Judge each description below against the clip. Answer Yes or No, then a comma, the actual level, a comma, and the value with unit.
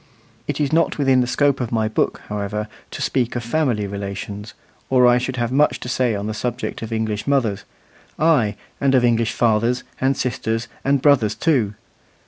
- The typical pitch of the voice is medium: No, low, 120 Hz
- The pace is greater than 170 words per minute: Yes, average, 185 wpm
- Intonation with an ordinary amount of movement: Yes, average, 3.7 semitones